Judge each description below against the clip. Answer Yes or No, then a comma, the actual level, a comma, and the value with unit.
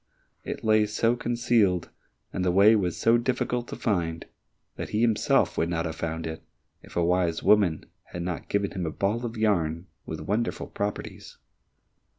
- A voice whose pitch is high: No, low, 100 Hz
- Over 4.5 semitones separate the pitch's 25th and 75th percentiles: Yes, average, 4.9 semitones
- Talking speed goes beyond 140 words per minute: Yes, average, 170 wpm